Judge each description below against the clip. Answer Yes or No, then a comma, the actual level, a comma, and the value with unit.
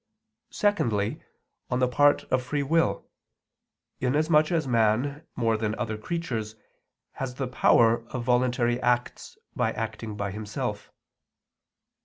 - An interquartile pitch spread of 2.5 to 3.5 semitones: No, average, 4.3 semitones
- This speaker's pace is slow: Yes, slow, 120 wpm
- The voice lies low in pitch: Yes, low, 125 Hz